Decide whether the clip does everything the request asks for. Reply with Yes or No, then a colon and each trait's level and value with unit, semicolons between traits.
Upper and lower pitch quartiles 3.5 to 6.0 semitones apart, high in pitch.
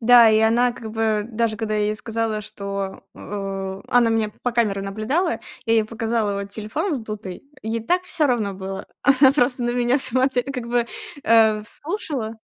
No: narrow, 2.6 semitones; high, 225 Hz